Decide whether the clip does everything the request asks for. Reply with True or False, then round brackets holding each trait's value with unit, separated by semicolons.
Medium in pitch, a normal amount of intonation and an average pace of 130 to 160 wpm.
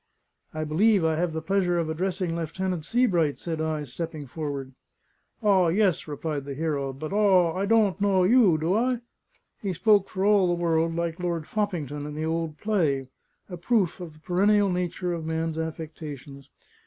False (170 Hz; 3.5 semitones; 175 wpm)